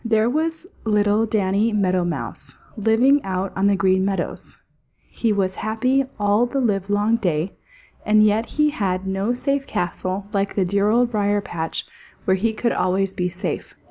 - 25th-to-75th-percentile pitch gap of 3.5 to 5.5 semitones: No, average, 3.1 semitones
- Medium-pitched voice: No, high, 205 Hz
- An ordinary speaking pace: Yes, average, 165 wpm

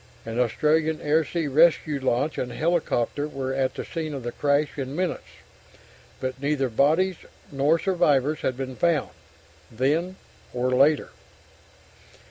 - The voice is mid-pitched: Yes, medium, 145 Hz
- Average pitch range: Yes, average, 3.3 semitones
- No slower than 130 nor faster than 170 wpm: Yes, slow, 135 wpm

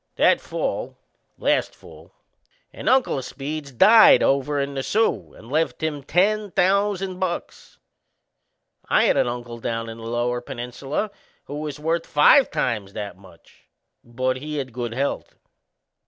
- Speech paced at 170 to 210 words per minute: No, average, 150 wpm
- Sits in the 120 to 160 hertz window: Yes, medium, 140 Hz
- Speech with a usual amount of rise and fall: No, wide, 5.7 semitones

